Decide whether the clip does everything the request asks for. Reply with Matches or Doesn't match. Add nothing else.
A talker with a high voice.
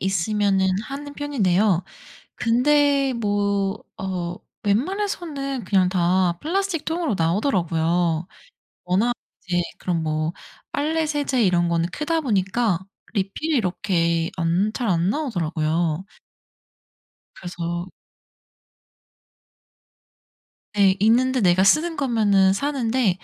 Matches